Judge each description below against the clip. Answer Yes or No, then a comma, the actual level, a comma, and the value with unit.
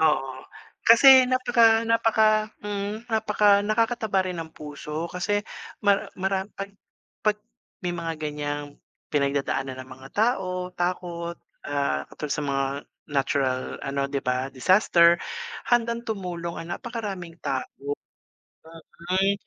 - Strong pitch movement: Yes, wide, 6.4 semitones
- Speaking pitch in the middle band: Yes, medium, 180 Hz